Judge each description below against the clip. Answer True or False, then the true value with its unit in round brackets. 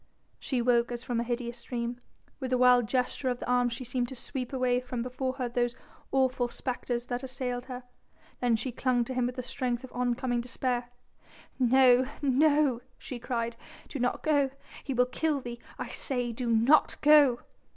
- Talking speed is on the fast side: False (185 wpm)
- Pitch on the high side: True (250 Hz)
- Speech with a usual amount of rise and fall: False (1.3 semitones)